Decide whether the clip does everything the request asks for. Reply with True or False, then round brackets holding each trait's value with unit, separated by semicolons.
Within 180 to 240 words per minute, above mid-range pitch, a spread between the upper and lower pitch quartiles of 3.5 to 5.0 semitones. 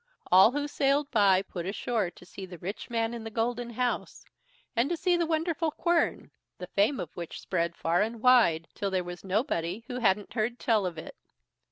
False (200 wpm; 220 Hz; 5.4 semitones)